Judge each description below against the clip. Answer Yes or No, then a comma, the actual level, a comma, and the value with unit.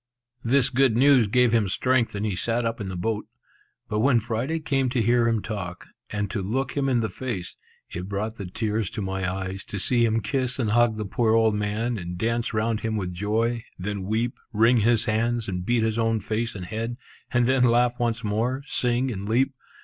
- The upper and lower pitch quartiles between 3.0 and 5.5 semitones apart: No, narrow, 2.6 semitones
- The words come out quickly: Yes, fast, 215 wpm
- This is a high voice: No, low, 115 Hz